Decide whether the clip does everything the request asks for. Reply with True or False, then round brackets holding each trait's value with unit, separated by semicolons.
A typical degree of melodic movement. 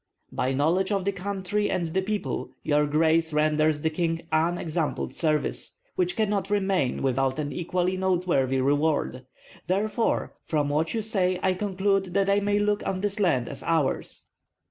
True (4.4 semitones)